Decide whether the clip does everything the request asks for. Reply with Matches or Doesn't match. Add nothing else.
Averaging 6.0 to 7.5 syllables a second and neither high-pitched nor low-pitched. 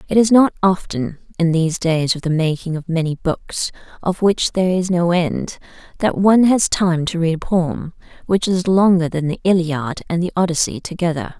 Doesn't match